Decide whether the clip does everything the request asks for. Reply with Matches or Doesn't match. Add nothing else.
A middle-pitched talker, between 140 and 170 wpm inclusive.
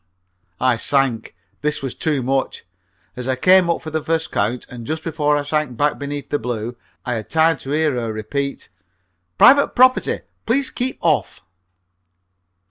Matches